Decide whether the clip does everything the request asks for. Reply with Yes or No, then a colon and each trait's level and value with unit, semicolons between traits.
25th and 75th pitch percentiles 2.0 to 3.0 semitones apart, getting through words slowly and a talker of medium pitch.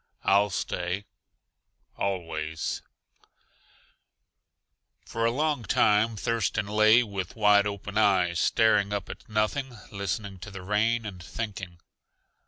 No: narrow, 2.6 semitones; slow, 110 wpm; low, 105 Hz